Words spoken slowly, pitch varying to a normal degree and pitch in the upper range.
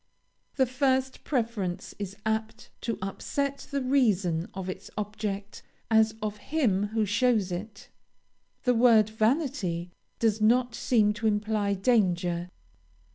Yes: slow, 125 wpm; average, 3.7 semitones; high, 215 Hz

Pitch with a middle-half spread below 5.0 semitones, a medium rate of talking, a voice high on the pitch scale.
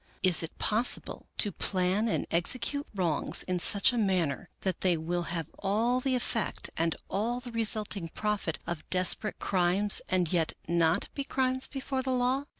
No: wide, 5.6 semitones; average, 165 wpm; high, 195 Hz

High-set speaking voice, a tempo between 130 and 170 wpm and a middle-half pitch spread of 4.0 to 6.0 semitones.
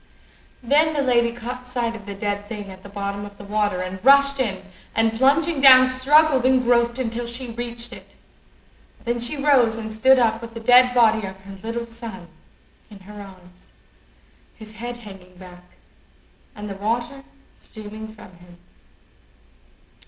No: high, 230 Hz; average, 165 wpm; average, 3.6 semitones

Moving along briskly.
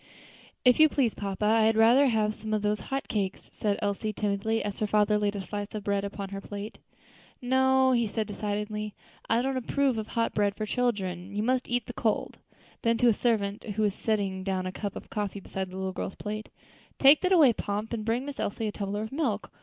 Yes: fast, 225 wpm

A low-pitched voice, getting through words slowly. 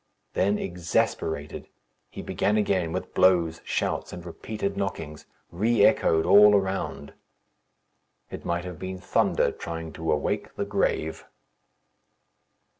Yes: very low, 90 Hz; slow, 115 wpm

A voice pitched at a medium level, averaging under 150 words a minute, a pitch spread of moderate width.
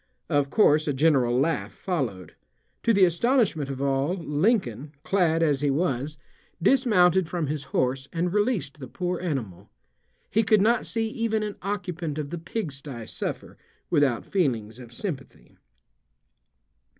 No: medium, 155 Hz; average, 140 wpm; wide, 5.7 semitones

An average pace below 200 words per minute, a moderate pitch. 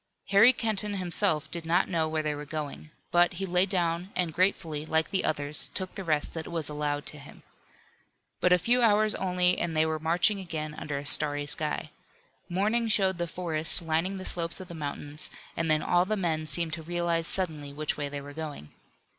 No: fast, 205 wpm; medium, 165 Hz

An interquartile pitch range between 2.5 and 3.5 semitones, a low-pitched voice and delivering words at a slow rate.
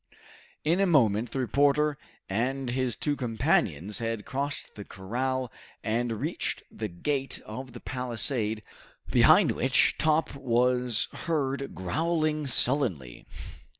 No: average, 4.0 semitones; low, 125 Hz; slow, 115 wpm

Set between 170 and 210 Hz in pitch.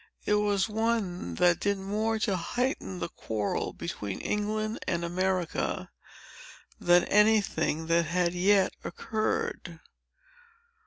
Yes: high, 190 Hz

